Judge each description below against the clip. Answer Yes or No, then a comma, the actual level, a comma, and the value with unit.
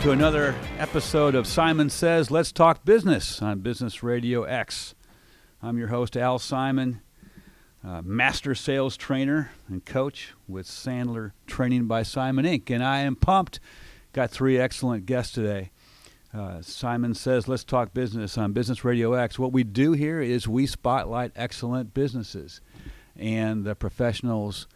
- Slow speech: No, average, 150 wpm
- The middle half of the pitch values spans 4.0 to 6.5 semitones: No, average, 3.2 semitones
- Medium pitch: No, low, 125 Hz